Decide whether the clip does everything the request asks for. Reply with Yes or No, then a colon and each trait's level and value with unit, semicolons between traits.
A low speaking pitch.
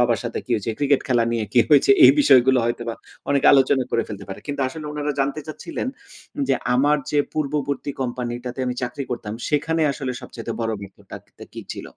Yes: low, 130 Hz